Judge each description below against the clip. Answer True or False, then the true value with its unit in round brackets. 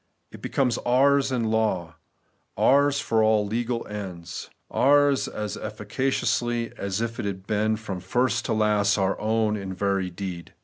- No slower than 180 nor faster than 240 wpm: False (150 wpm)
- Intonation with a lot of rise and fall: False (3.4 semitones)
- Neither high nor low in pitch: False (110 Hz)